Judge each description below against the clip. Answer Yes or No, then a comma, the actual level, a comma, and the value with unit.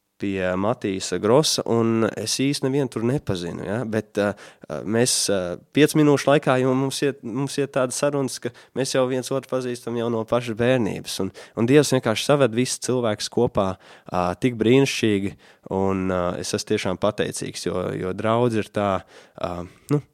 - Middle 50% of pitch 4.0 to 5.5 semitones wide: Yes, average, 4.3 semitones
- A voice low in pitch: Yes, low, 115 Hz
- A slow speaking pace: No, average, 155 wpm